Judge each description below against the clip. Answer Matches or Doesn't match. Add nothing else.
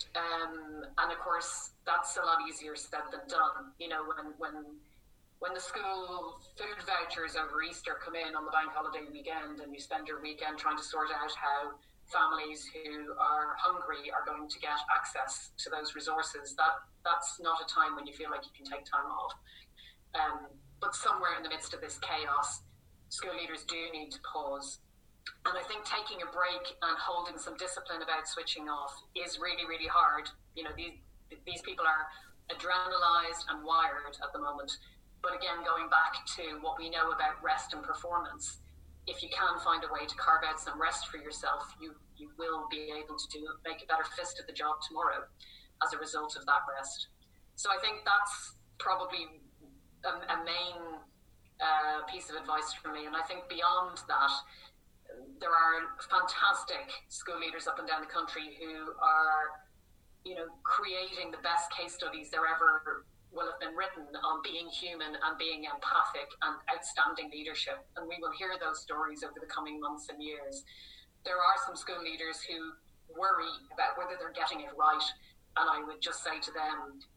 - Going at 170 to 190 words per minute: Matches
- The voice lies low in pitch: Doesn't match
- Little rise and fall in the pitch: Matches